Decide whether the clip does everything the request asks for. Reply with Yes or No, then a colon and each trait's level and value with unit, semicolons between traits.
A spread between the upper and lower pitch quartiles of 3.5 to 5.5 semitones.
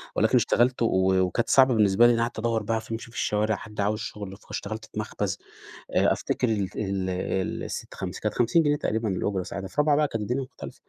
No: average, 2.9 semitones